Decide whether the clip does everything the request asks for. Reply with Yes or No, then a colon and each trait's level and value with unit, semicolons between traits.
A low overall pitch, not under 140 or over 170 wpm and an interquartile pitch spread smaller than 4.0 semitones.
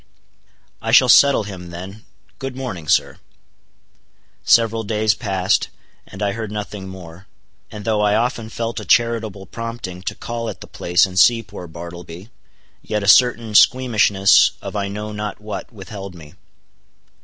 Yes: low, 105 Hz; average, 150 wpm; average, 3.3 semitones